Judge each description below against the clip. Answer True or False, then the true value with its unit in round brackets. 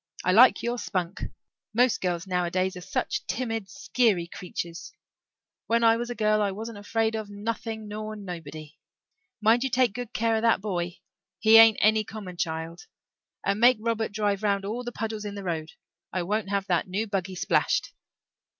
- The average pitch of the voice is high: True (210 Hz)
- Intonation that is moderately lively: True (3.6 semitones)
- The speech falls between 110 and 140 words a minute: False (175 wpm)